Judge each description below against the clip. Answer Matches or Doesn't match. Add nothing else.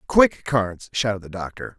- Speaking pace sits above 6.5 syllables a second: Doesn't match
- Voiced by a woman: Doesn't match